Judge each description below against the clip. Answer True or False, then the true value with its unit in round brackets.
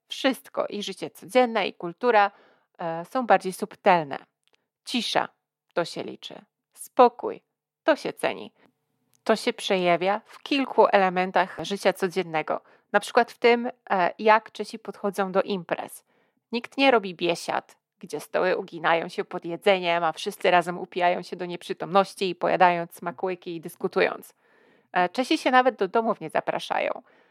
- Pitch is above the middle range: True (195 Hz)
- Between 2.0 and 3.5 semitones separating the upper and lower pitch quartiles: False (4.1 semitones)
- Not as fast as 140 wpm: False (145 wpm)